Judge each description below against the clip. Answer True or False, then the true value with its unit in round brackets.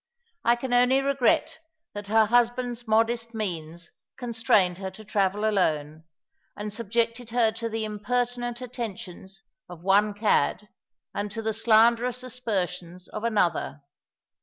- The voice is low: False (220 Hz)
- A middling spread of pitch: True (3.5 semitones)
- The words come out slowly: True (130 wpm)